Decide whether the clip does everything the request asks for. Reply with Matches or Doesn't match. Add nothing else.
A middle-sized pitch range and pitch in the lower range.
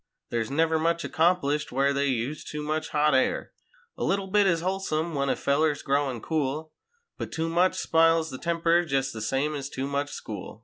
Doesn't match